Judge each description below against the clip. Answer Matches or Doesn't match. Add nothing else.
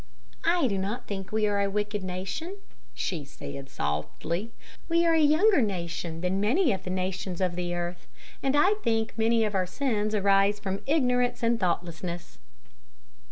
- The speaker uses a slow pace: Doesn't match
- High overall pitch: Matches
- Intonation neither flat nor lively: Matches